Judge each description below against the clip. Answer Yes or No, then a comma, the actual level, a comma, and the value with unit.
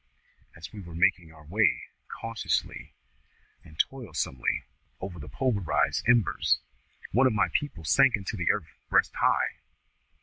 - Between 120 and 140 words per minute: Yes, slow, 135 wpm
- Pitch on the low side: Yes, very low, 95 Hz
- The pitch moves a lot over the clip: Yes, wide, 5.8 semitones